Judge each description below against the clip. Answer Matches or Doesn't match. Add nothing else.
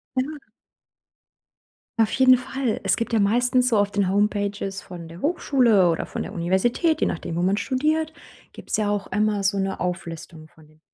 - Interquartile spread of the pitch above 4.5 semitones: Matches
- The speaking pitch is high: Matches